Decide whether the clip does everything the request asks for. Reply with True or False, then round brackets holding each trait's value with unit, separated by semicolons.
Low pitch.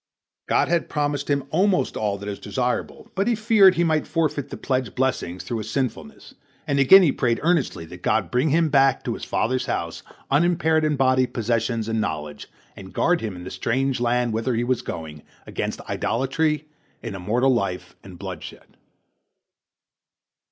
True (130 Hz)